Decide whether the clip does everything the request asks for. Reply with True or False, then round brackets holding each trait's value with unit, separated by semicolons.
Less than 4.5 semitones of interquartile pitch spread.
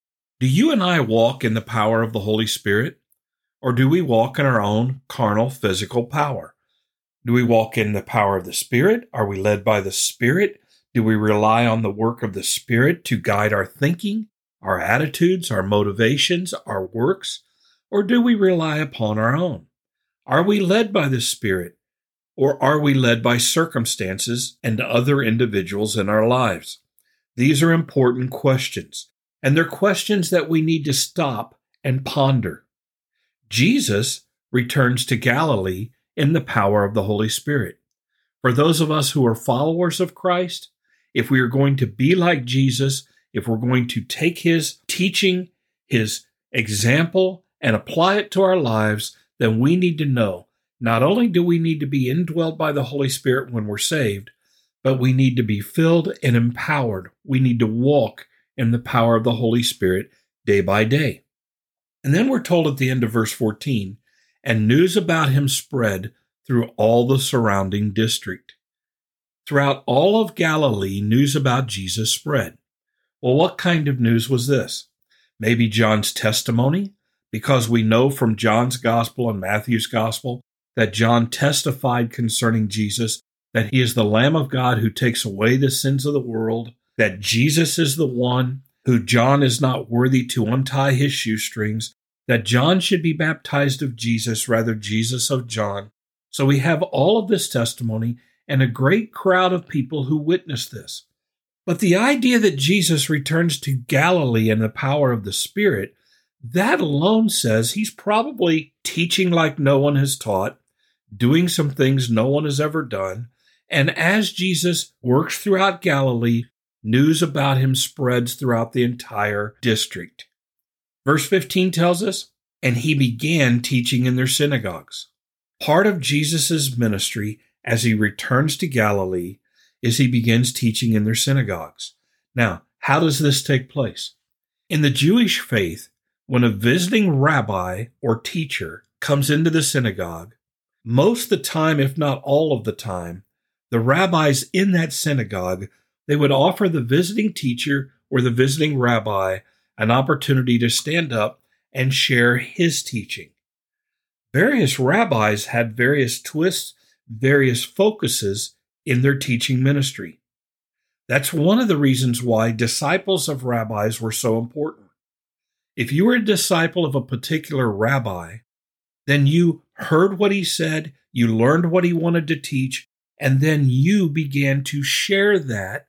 False (5.4 semitones)